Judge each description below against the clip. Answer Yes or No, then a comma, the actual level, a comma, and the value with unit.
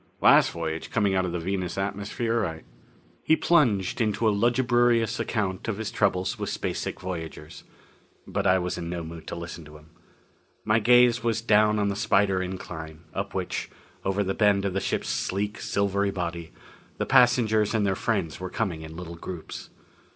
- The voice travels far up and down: No, average, 4.1 semitones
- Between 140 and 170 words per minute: No, average, 180 wpm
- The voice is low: Yes, low, 100 Hz